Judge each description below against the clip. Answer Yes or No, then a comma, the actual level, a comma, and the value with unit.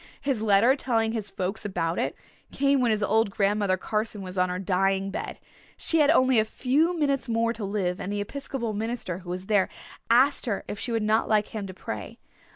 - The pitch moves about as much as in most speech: Yes, average, 3.8 semitones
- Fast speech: Yes, fast, 210 wpm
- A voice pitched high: Yes, high, 215 Hz